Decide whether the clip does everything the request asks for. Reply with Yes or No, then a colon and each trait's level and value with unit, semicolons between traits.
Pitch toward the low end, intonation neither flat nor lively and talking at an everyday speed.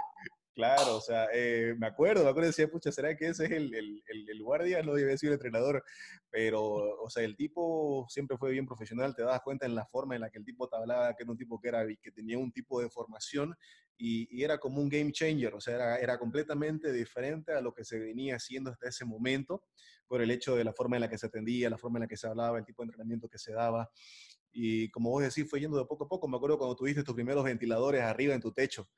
No: low, 125 Hz; average, 3.9 semitones; fast, 265 wpm